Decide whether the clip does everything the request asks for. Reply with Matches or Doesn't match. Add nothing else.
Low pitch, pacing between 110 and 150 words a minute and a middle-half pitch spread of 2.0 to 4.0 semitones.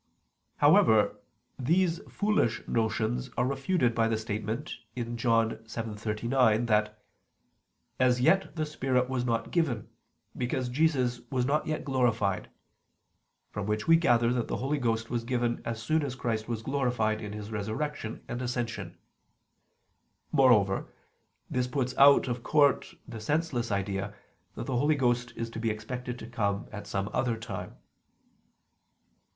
Matches